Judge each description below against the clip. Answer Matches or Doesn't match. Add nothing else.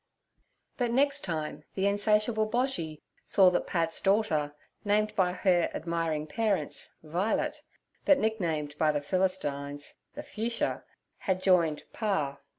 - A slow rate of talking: Matches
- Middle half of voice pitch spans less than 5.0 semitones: Doesn't match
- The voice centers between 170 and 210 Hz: Matches